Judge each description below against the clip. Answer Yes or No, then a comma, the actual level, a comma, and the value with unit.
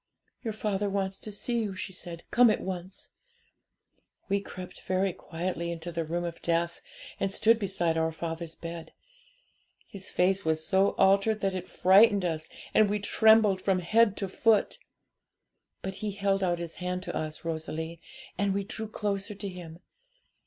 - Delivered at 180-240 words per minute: No, average, 165 wpm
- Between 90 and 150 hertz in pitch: No, high, 190 Hz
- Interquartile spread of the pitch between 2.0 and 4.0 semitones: Yes, average, 2.9 semitones